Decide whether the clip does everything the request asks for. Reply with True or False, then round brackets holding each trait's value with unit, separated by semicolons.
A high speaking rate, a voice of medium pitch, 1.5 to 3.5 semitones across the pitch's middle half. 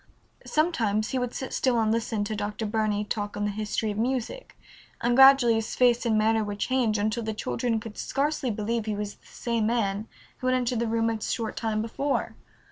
False (210 wpm; 225 Hz; 2.4 semitones)